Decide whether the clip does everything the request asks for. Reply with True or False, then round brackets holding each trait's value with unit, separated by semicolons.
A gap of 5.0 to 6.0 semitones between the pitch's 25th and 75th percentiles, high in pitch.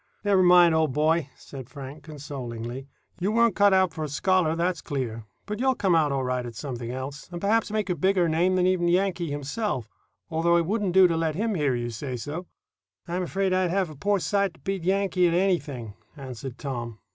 False (5.3 semitones; 165 Hz)